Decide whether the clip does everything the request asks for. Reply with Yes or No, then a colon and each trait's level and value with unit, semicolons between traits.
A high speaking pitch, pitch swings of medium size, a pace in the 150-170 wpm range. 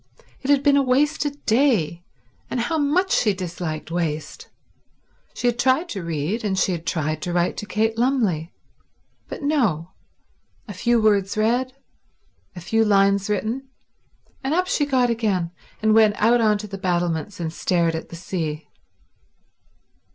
No: high, 210 Hz; wide, 6.4 semitones; average, 155 wpm